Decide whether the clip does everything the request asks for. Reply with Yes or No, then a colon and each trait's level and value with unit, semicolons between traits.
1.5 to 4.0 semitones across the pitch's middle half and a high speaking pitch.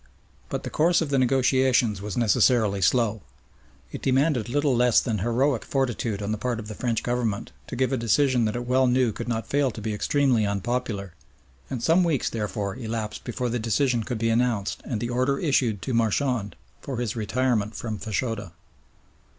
No: average, 3.2 semitones; low, 120 Hz